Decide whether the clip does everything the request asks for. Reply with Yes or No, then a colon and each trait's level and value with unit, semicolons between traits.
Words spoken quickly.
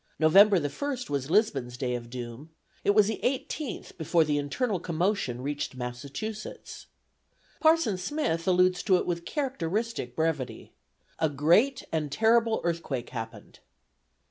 No: slow, 135 wpm